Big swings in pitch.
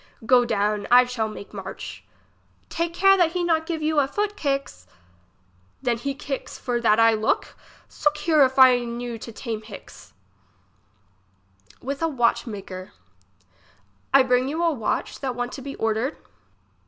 No: average, 4.7 semitones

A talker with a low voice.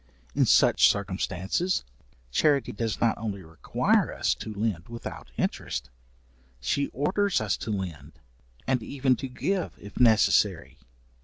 Yes: low, 110 Hz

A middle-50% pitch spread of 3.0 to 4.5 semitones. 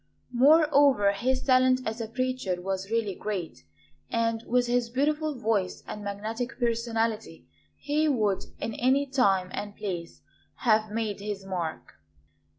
Yes: average, 4.2 semitones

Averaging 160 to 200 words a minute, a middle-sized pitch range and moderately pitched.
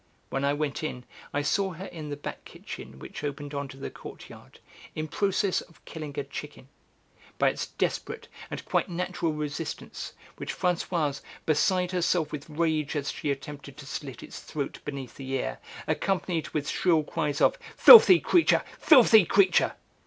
Yes: average, 165 wpm; average, 3.9 semitones; medium, 150 Hz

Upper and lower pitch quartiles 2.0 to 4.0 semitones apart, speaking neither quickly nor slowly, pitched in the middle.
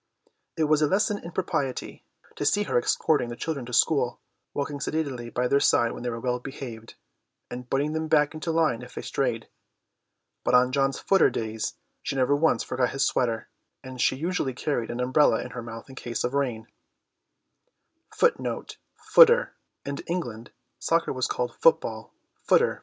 No: average, 3.7 semitones; average, 145 wpm; low, 130 Hz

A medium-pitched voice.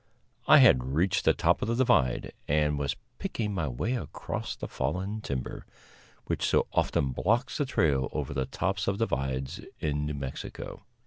No: very low, 75 Hz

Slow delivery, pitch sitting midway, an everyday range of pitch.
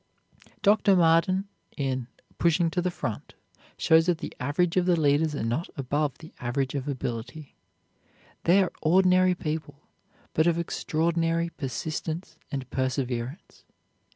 Yes: slow, 130 wpm; medium, 160 Hz; average, 3.9 semitones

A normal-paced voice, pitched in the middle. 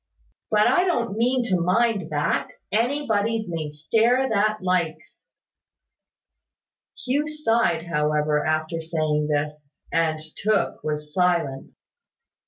No: slow, 105 wpm; medium, 180 Hz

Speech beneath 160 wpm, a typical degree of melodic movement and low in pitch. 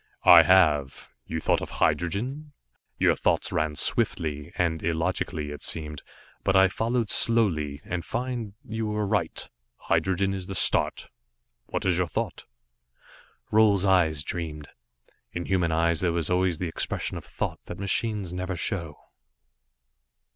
Yes: average, 140 wpm; average, 3.7 semitones; very low, 90 Hz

